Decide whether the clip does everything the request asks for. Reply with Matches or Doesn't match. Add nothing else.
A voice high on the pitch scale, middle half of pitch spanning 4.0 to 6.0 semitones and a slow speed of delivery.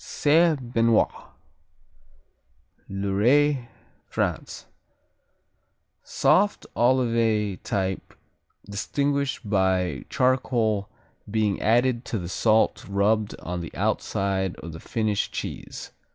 Doesn't match